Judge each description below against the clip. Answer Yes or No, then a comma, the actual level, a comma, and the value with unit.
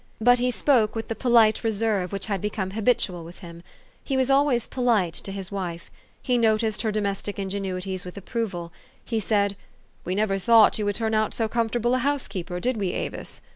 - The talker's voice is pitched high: Yes, high, 215 Hz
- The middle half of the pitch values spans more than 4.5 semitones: No, average, 3.4 semitones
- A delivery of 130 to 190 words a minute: No, fast, 205 wpm